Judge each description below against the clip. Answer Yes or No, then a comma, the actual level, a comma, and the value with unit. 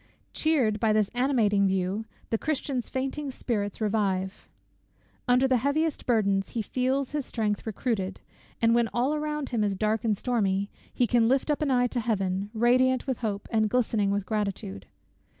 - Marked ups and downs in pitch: No, average, 4.1 semitones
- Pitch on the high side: Yes, high, 225 Hz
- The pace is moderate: Yes, average, 170 wpm